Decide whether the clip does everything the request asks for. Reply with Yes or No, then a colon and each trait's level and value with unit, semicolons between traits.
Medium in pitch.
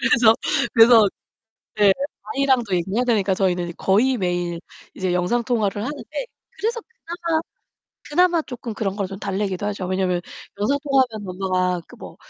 No: high, 205 Hz